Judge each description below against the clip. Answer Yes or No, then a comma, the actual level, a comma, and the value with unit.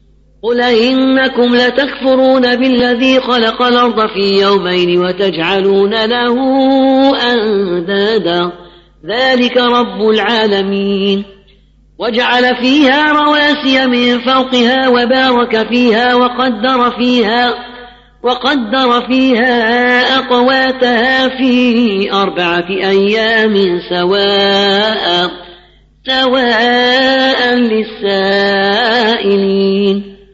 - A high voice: Yes, high, 240 Hz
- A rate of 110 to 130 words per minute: No, slow, 65 wpm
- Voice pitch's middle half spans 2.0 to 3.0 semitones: No, average, 4.2 semitones